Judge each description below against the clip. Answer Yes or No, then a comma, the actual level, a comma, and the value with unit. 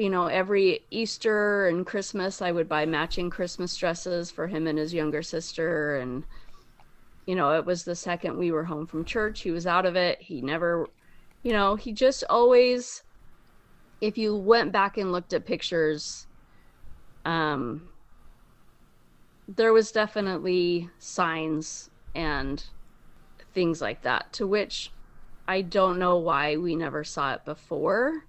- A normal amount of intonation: Yes, average, 4.0 semitones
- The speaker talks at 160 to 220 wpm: No, average, 150 wpm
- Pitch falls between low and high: Yes, medium, 175 Hz